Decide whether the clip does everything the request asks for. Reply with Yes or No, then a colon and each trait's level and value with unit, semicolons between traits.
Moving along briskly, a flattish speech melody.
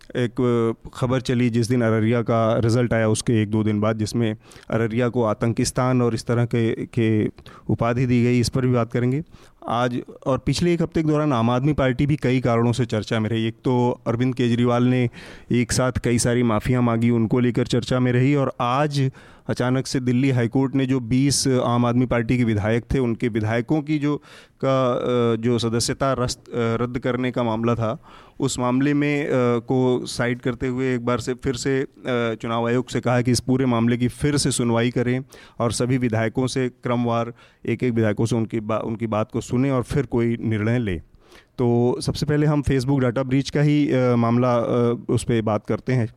Yes: fast, 200 wpm; narrow, 2.0 semitones